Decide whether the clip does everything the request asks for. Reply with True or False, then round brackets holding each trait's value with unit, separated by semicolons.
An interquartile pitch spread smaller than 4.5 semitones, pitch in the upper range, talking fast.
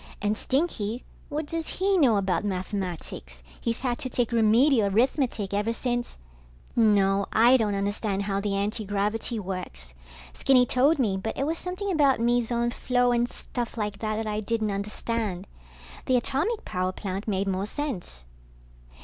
False (3.9 semitones; 220 Hz; 155 wpm)